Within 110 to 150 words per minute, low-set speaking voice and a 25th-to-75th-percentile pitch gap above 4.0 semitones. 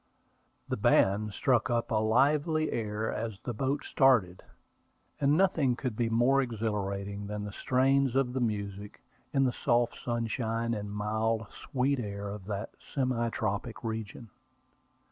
No: average, 145 wpm; low, 115 Hz; average, 3.7 semitones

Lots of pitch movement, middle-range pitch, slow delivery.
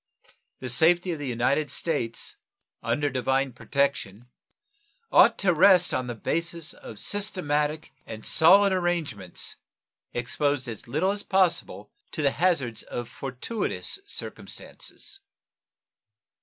Yes: wide, 6.0 semitones; medium, 145 Hz; slow, 115 wpm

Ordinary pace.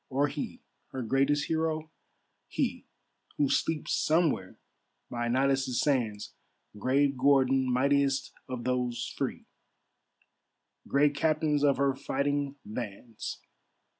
No: slow, 105 wpm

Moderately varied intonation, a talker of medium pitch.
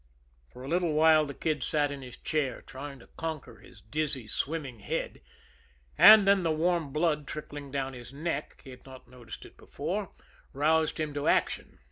Yes: average, 3.2 semitones; medium, 145 Hz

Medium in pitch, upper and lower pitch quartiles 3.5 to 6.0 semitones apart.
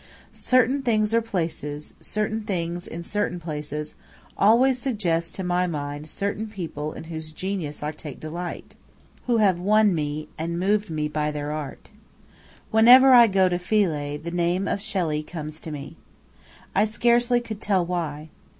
Yes: medium, 175 Hz; wide, 5.6 semitones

